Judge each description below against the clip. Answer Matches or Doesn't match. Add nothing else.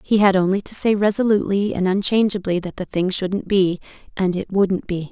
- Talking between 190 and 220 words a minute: Matches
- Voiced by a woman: Matches